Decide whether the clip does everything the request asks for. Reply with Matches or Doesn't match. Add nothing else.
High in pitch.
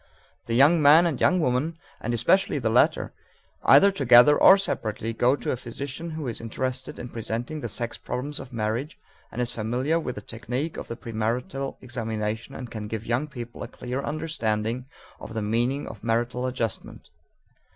Doesn't match